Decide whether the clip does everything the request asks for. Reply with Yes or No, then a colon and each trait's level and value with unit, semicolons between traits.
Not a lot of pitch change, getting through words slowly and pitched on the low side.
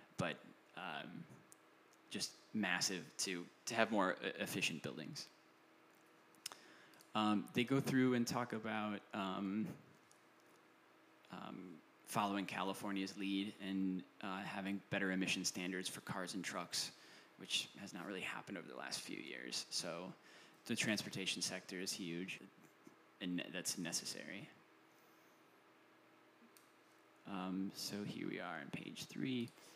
Yes: narrow, 2.3 semitones; slow, 120 wpm; low, 100 Hz